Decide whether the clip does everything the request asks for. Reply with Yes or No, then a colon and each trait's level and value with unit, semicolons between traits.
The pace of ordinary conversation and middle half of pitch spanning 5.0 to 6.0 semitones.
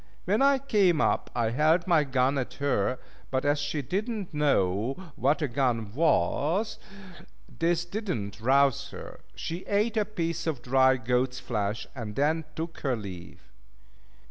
Yes: average, 160 wpm; wide, 5.6 semitones